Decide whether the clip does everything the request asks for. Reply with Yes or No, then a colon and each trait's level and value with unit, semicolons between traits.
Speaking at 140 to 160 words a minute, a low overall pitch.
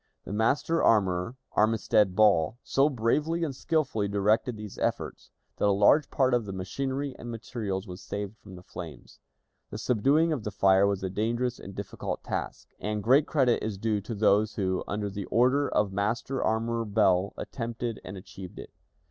No: average, 175 wpm; low, 110 Hz